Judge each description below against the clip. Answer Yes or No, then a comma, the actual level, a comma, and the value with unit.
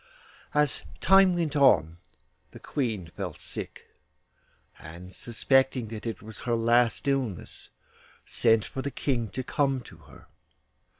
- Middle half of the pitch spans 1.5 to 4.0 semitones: No, average, 4.5 semitones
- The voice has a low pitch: Yes, low, 120 Hz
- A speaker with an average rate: No, slow, 130 wpm